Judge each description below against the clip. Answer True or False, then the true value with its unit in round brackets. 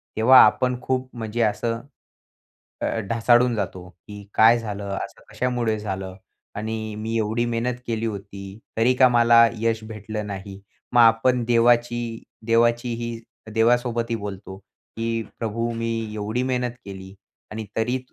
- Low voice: True (115 Hz)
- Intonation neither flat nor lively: False (1.9 semitones)